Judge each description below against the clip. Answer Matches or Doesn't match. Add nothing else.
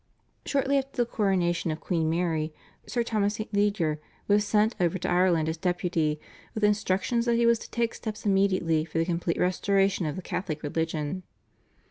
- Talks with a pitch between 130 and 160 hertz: Doesn't match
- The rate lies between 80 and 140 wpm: Doesn't match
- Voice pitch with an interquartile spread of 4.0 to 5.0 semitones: Matches